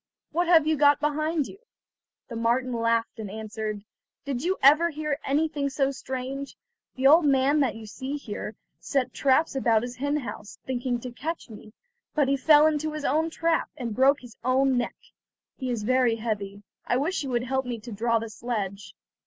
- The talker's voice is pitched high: Yes, very high, 260 Hz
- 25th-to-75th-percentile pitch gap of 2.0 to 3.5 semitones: No, average, 4.1 semitones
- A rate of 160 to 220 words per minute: Yes, average, 190 wpm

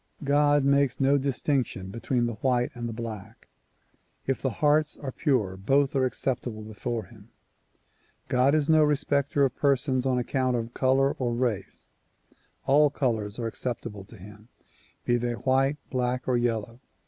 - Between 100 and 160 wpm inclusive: Yes, average, 150 wpm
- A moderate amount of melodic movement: Yes, average, 3.0 semitones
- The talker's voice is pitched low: Yes, low, 125 Hz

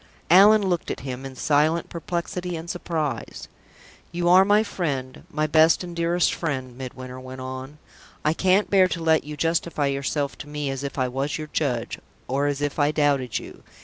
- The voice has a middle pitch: Yes, medium, 150 Hz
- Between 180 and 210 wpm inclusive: Yes, average, 185 wpm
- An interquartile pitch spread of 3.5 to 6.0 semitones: Yes, average, 4.1 semitones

